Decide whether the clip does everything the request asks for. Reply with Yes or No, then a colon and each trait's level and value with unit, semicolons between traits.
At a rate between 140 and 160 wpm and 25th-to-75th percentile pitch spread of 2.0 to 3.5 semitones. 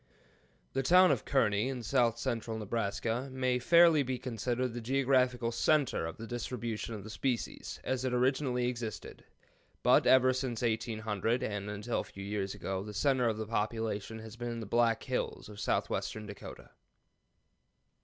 Yes: average, 155 wpm; average, 2.8 semitones